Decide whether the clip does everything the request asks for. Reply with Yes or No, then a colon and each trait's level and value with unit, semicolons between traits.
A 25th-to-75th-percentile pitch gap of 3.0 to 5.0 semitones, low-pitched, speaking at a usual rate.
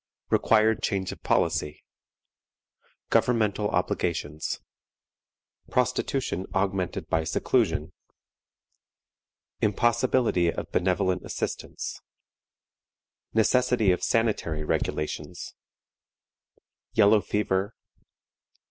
No: average, 4.0 semitones; low, 100 Hz; slow, 65 wpm